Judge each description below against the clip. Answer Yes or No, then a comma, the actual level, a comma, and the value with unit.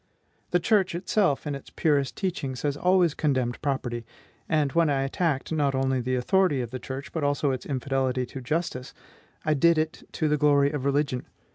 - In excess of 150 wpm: Yes, average, 185 wpm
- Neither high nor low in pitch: Yes, medium, 145 Hz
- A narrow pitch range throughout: No, average, 3.2 semitones